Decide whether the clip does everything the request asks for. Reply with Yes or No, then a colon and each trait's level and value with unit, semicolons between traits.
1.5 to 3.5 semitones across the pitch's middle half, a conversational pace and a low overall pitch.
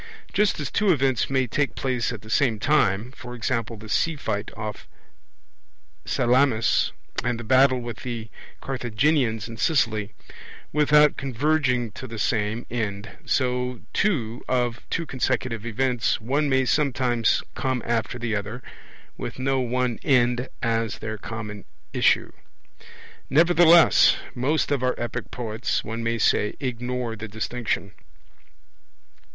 No: average, 2.9 semitones; slow, 130 wpm; low, 125 Hz